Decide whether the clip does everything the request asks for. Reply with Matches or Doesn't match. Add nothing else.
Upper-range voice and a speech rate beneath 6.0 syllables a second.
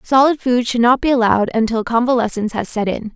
Doesn't match